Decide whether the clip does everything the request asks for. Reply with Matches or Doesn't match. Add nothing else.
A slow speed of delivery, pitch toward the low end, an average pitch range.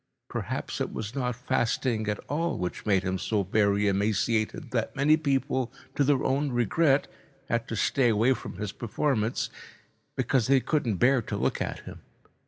Doesn't match